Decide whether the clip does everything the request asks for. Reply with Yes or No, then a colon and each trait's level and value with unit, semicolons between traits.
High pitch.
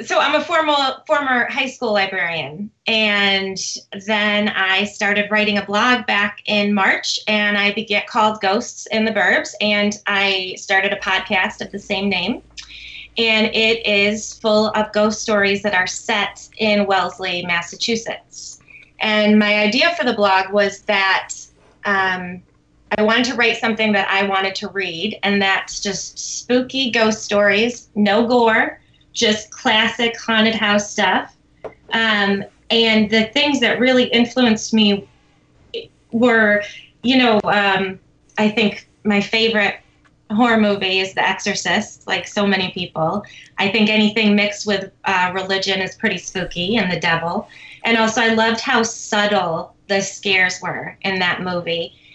Yes: high, 205 Hz